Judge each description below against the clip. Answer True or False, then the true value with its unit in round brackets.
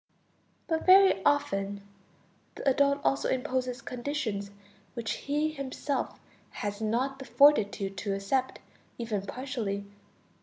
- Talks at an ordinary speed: False (110 wpm)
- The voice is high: True (255 Hz)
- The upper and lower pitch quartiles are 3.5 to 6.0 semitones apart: True (5.6 semitones)